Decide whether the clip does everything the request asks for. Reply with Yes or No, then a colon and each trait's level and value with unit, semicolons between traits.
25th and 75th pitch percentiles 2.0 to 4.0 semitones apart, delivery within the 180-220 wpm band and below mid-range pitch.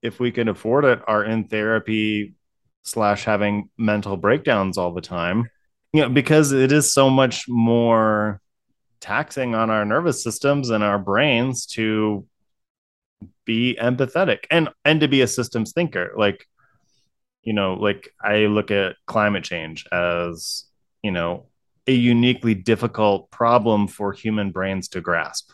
No: average, 3.3 semitones; average, 145 wpm; low, 110 Hz